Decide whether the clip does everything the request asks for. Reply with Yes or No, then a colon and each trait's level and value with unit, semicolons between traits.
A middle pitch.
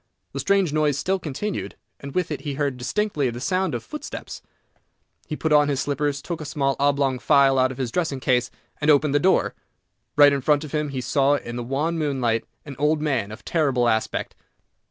Yes: medium, 145 Hz